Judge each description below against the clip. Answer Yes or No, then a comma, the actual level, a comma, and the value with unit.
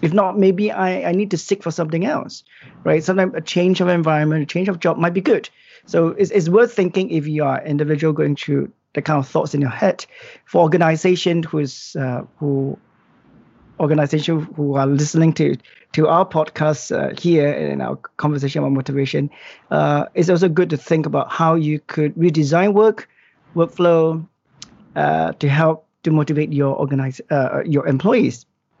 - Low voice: No, medium, 160 Hz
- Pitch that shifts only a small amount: No, average, 3.5 semitones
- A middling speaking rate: Yes, average, 180 wpm